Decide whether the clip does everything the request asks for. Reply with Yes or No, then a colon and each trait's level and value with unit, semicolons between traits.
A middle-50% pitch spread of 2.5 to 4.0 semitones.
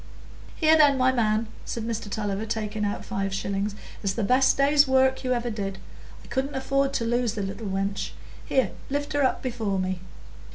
No: average, 4.6 semitones